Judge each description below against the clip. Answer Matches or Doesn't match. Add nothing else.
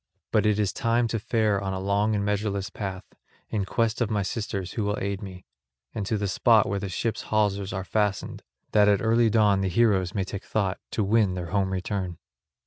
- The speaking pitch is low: Matches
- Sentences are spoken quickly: Matches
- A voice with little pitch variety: Matches